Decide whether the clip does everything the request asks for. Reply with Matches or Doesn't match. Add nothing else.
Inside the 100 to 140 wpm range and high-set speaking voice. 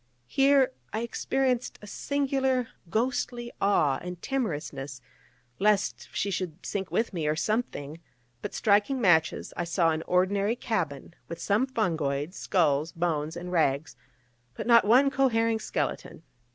Matches